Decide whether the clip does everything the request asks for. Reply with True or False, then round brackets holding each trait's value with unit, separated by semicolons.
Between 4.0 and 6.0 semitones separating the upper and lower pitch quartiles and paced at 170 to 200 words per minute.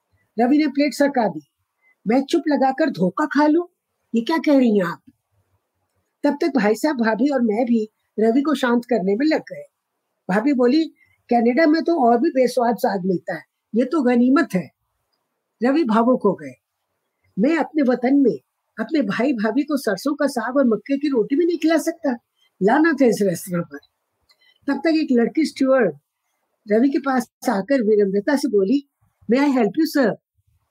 True (4.8 semitones; 180 wpm)